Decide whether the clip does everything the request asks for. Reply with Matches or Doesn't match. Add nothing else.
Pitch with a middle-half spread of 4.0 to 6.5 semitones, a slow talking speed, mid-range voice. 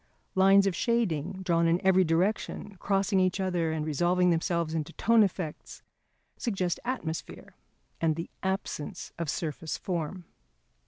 Doesn't match